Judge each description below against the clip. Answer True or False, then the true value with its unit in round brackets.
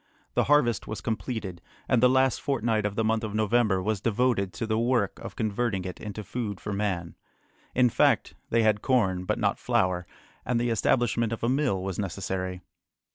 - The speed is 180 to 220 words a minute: True (185 wpm)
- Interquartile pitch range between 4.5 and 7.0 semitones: False (3.5 semitones)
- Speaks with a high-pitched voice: False (110 Hz)